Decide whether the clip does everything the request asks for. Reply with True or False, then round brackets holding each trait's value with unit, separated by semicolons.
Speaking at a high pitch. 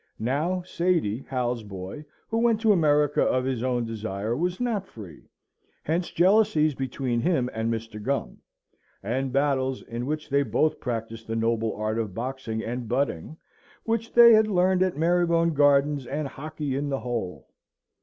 False (135 Hz)